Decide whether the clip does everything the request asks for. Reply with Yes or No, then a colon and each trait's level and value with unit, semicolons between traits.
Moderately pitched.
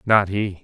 No: low, 100 Hz